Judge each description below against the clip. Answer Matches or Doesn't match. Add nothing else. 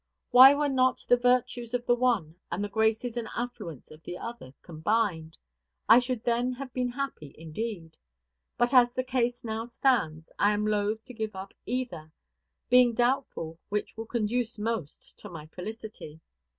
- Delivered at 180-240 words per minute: Doesn't match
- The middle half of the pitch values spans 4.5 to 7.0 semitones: Doesn't match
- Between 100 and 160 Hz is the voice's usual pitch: Doesn't match